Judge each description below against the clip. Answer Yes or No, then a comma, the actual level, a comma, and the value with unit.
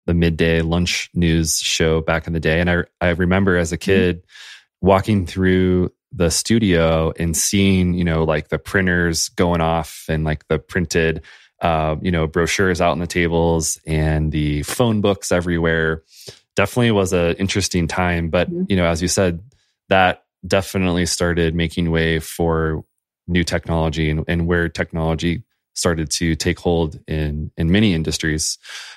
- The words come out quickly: No, average, 160 wpm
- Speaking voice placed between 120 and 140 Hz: No, very low, 85 Hz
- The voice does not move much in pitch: Yes, narrow, 2.0 semitones